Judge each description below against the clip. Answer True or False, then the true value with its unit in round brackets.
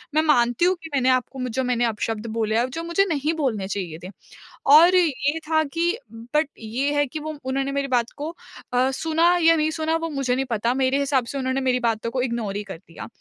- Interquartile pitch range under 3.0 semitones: False (4.7 semitones)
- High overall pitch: True (265 Hz)